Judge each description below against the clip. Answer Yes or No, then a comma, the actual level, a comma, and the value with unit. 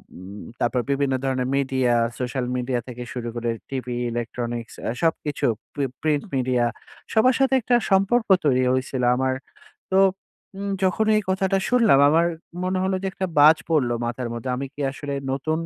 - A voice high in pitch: No, low, 135 Hz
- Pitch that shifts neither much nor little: No, wide, 6.7 semitones